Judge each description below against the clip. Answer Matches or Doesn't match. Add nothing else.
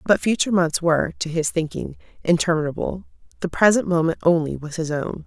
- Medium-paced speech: Matches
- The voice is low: Doesn't match